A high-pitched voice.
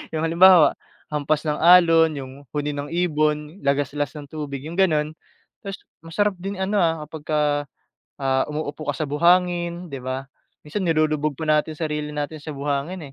No: medium, 155 Hz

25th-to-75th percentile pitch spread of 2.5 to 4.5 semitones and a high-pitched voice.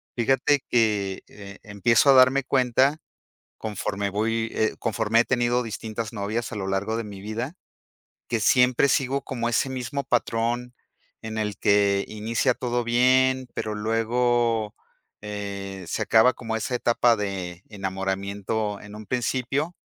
No: average, 3.1 semitones; low, 115 Hz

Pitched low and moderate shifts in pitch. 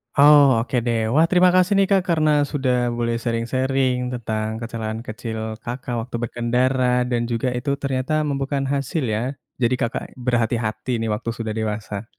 Yes: low, 125 Hz; average, 3.1 semitones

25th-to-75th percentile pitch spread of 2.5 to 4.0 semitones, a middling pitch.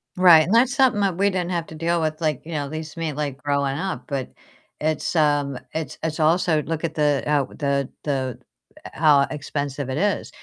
Yes: average, 2.9 semitones; medium, 155 Hz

